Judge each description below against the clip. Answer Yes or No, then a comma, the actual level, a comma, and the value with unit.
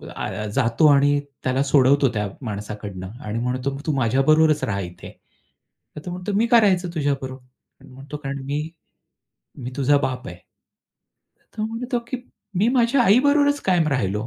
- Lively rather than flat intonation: Yes, wide, 6.5 semitones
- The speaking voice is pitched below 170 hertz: Yes, medium, 140 Hz